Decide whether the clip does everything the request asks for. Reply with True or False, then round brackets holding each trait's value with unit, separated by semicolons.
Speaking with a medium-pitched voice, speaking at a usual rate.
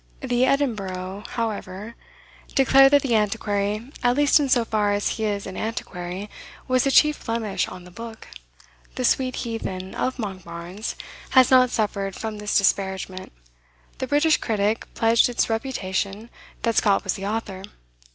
False (220 Hz; 150 wpm)